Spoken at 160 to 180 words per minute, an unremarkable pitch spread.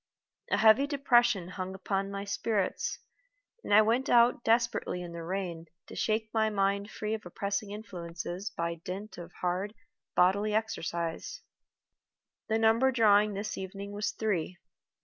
No: average, 145 wpm; average, 3.2 semitones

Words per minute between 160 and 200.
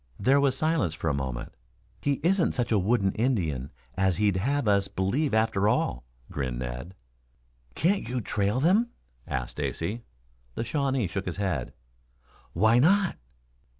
No: average, 150 wpm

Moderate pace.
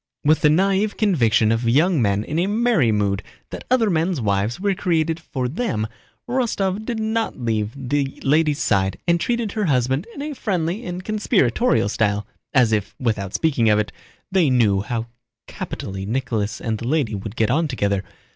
Yes: average, 175 wpm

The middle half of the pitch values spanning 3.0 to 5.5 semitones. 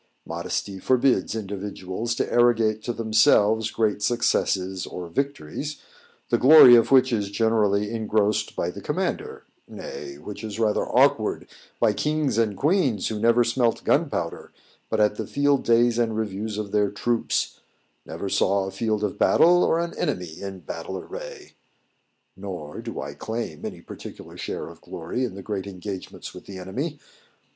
Yes: average, 3.8 semitones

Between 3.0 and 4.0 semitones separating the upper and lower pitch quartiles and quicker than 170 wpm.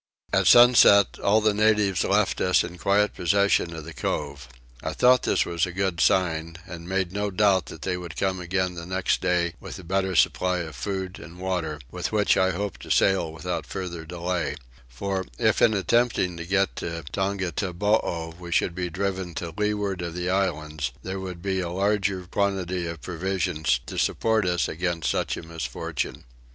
No: narrow, 2.6 semitones; average, 180 wpm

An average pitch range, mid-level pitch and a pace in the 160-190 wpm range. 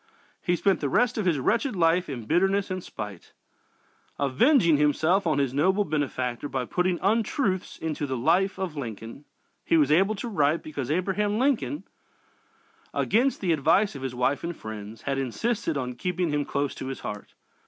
No: wide, 6.0 semitones; medium, 160 Hz; average, 175 wpm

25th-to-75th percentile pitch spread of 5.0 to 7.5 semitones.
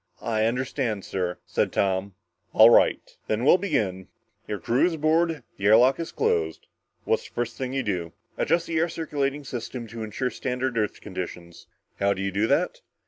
Yes: wide, 5.6 semitones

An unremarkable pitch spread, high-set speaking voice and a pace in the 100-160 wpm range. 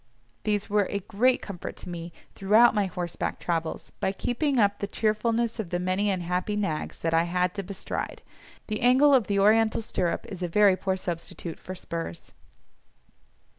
No: average, 3.2 semitones; high, 200 Hz; average, 170 wpm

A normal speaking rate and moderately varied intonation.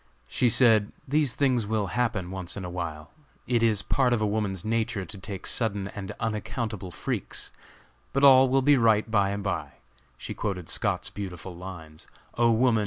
Yes: average, 175 wpm; average, 3.9 semitones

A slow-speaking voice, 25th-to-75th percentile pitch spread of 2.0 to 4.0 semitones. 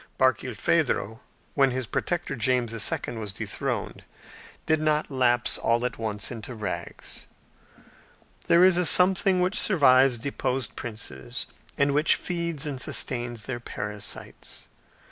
No: slow, 125 wpm; average, 5.0 semitones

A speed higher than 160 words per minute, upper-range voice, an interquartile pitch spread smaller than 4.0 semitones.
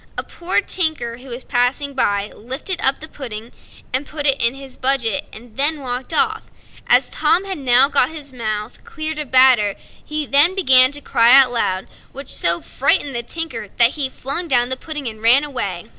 Yes: average, 185 wpm; very high, 265 Hz; average, 3.6 semitones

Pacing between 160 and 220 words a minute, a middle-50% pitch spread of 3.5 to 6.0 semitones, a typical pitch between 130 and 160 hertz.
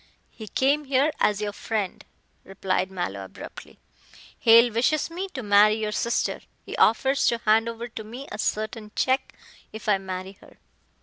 No: average, 165 wpm; average, 3.8 semitones; high, 220 Hz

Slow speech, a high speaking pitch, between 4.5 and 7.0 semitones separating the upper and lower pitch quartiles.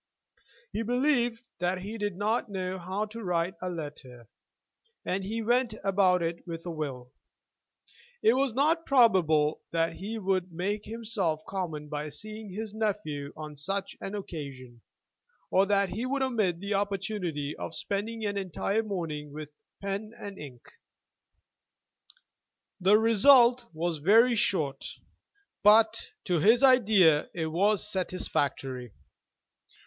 Yes: slow, 130 wpm; high, 195 Hz; average, 5.1 semitones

